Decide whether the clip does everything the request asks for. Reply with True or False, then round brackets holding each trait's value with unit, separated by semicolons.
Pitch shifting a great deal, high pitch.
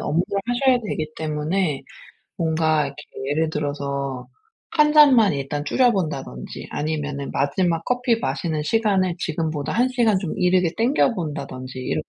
False (6.3 semitones; 160 Hz)